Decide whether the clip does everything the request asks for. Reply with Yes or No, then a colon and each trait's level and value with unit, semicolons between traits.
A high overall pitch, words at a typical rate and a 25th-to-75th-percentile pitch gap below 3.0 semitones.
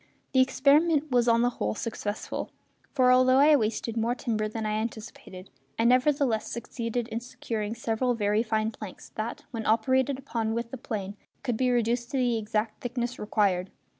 Yes: high, 230 Hz; average, 170 wpm; narrow, 2.6 semitones